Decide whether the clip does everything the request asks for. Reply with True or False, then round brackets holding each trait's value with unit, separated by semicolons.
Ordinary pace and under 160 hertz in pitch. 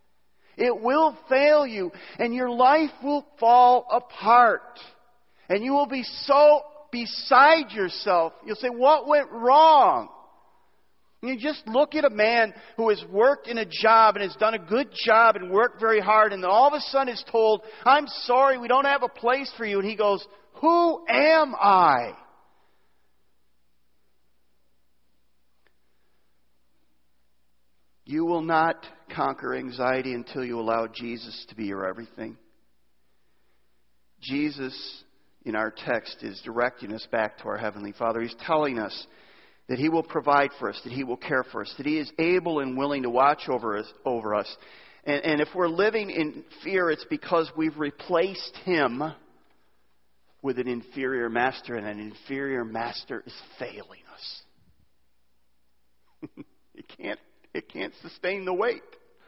False (150 wpm; 170 Hz)